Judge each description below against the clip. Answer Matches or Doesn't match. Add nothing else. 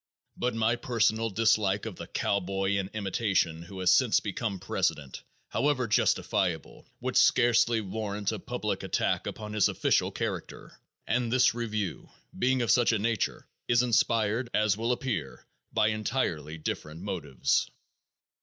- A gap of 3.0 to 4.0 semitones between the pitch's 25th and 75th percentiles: Matches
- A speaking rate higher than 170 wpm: Doesn't match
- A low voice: Matches